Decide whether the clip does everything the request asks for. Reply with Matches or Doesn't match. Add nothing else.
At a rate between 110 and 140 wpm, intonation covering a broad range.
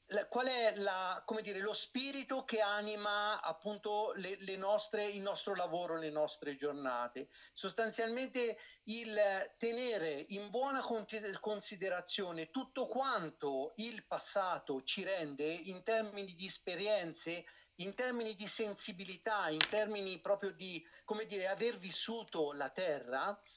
Doesn't match